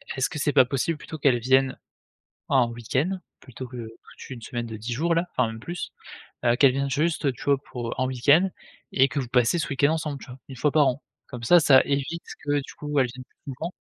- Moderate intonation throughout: Yes, average, 3.0 semitones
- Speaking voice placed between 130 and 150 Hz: Yes, low, 135 Hz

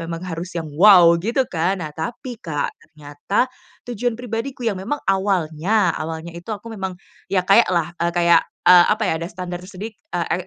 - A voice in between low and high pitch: Yes, medium, 180 Hz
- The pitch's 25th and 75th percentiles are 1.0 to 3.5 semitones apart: No, average, 4.2 semitones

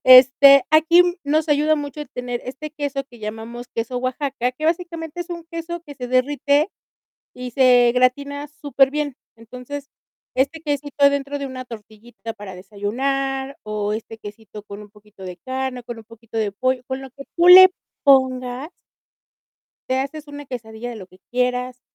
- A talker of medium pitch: No, very high, 260 Hz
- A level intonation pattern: No, average, 3.4 semitones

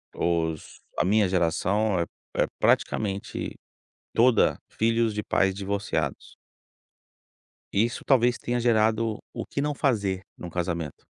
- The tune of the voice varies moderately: Yes, average, 4.2 semitones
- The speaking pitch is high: No, low, 105 Hz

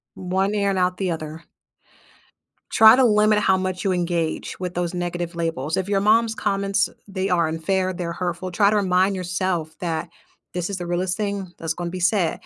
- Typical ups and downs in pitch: No, narrow, 2.3 semitones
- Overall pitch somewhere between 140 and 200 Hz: Yes, medium, 185 Hz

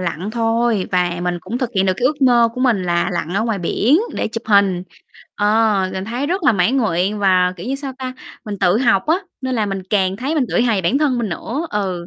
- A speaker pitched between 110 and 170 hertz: No, high, 215 Hz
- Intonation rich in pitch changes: No, average, 4.9 semitones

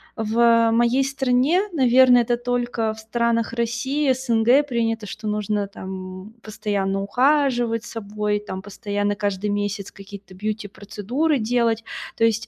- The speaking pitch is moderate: No, high, 225 Hz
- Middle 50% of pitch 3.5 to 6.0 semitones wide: No, average, 2.9 semitones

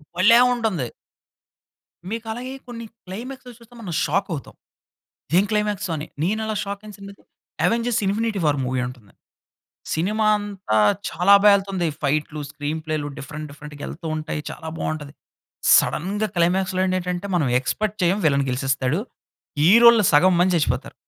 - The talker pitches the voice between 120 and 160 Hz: No, medium, 185 Hz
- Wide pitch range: Yes, wide, 5.7 semitones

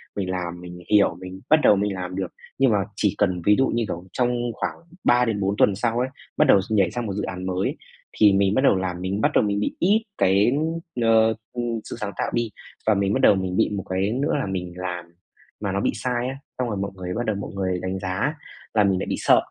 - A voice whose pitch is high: No, low, 100 Hz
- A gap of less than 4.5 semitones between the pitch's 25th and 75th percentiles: Yes, average, 3.7 semitones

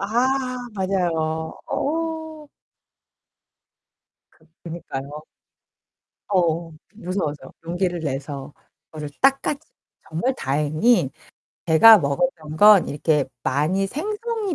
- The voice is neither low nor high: Yes, medium, 175 Hz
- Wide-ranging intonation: Yes, wide, 8.6 semitones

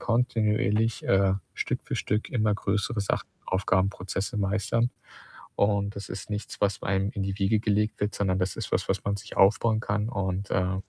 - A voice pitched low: Yes, low, 100 Hz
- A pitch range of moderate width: No, narrow, 1.7 semitones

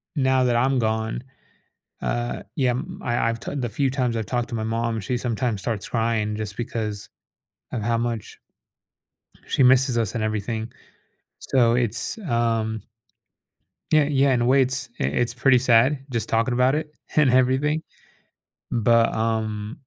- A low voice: Yes, low, 120 Hz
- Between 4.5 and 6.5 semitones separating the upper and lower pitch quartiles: No, narrow, 2.6 semitones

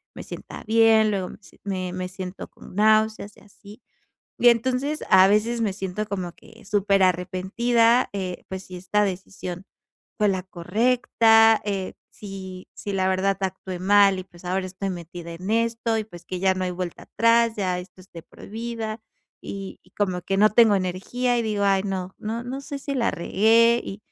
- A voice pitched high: Yes, high, 200 Hz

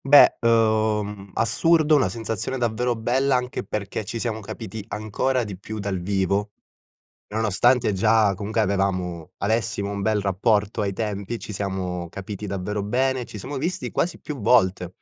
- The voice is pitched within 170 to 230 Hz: No, low, 105 Hz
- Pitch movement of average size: Yes, average, 3.2 semitones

